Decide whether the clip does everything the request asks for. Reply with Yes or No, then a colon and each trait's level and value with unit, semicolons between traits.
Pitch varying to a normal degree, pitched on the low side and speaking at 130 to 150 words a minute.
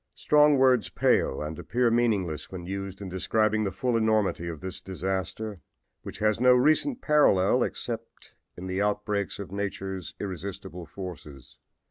Yes: average, 3.2 semitones; low, 100 Hz; average, 145 wpm